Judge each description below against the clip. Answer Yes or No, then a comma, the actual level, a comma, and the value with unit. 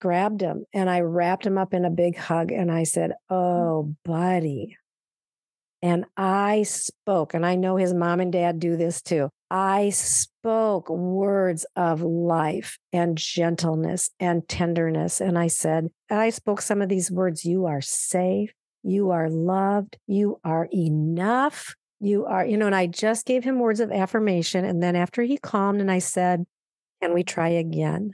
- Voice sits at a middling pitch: Yes, medium, 180 Hz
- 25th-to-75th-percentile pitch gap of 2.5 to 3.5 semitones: Yes, average, 2.8 semitones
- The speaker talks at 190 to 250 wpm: No, average, 175 wpm